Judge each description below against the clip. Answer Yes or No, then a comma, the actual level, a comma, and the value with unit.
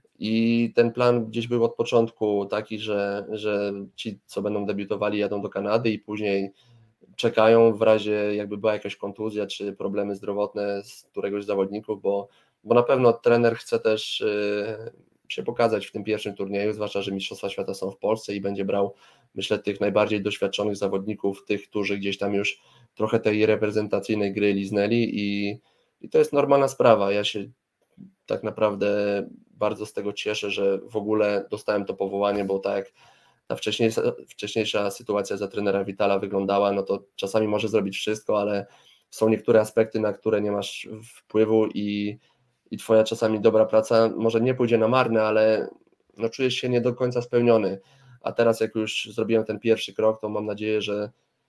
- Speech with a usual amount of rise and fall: No, narrow, 1.7 semitones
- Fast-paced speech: Yes, fast, 170 wpm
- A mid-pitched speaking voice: No, low, 105 Hz